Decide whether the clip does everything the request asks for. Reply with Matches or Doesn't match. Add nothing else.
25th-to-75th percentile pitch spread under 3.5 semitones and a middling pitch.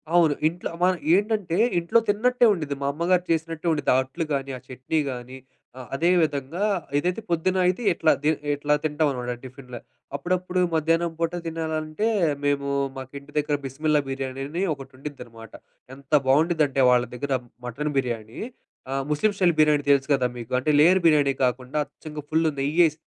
Doesn't match